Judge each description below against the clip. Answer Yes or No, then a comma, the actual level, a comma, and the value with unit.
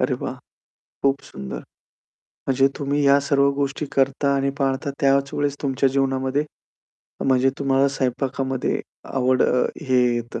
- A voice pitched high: No, low, 135 Hz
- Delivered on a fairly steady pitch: Yes, narrow, 1.0 semitones